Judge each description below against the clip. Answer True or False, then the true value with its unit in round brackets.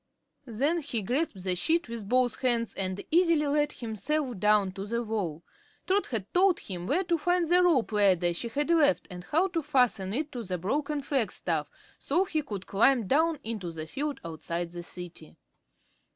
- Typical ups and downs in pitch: False (8.0 semitones)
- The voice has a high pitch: True (240 Hz)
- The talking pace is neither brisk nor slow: True (180 wpm)